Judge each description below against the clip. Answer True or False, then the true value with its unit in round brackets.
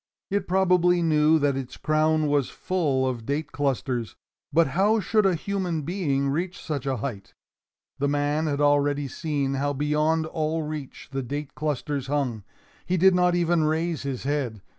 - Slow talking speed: False (165 wpm)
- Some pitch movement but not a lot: True (3.2 semitones)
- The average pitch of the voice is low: False (150 Hz)